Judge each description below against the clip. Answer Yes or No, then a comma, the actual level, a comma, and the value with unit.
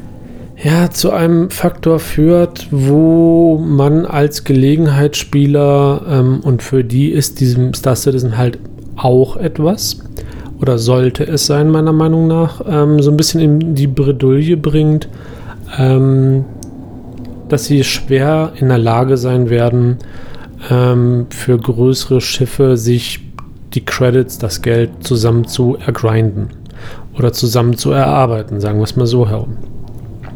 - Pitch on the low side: Yes, low, 130 Hz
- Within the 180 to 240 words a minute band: No, average, 130 wpm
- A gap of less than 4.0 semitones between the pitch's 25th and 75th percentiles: Yes, average, 3.4 semitones